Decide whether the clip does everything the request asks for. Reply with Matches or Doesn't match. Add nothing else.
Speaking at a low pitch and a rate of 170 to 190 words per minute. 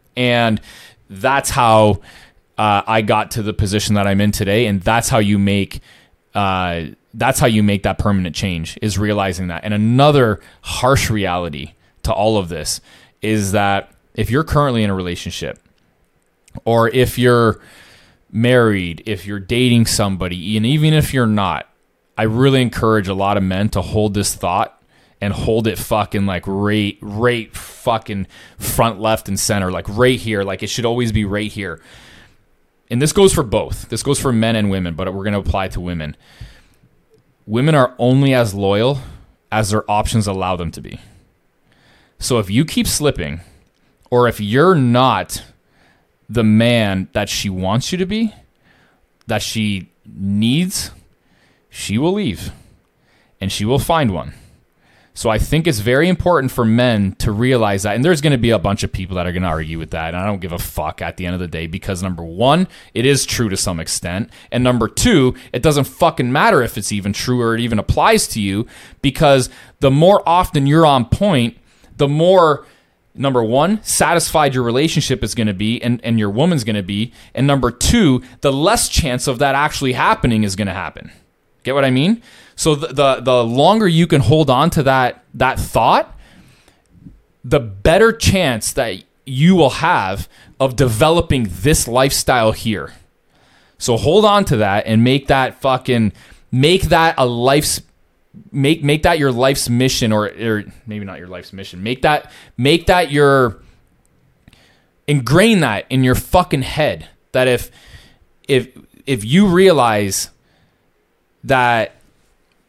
Matches